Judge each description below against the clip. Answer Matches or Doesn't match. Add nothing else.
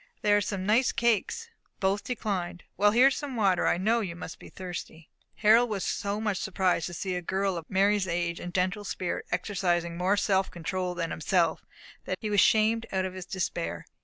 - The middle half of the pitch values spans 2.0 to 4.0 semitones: Matches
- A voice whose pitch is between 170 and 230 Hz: Matches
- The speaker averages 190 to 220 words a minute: Matches